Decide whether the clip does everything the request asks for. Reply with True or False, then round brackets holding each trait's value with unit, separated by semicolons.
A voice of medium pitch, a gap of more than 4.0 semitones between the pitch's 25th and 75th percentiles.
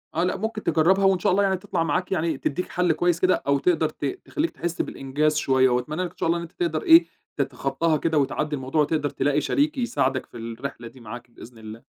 True (155 Hz; 5.0 semitones)